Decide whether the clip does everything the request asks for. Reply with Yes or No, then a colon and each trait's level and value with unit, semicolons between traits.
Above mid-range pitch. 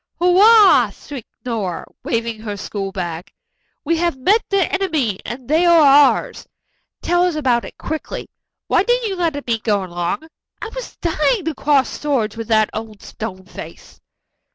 Yes: very high, 275 Hz